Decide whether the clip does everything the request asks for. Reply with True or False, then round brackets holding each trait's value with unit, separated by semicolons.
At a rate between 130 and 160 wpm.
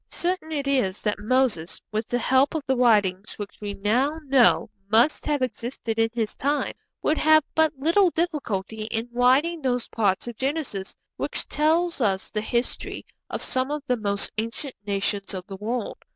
False (175 wpm)